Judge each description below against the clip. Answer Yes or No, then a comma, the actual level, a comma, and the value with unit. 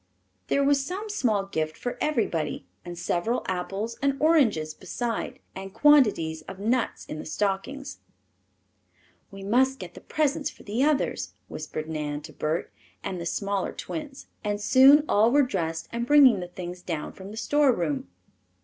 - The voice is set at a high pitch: Yes, high, 205 Hz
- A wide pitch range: Yes, wide, 7.8 semitones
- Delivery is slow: No, average, 160 wpm